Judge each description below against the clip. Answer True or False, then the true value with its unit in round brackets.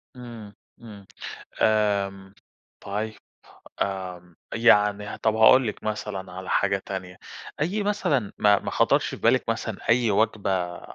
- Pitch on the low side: True (105 Hz)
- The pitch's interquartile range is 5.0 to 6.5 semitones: False (2.4 semitones)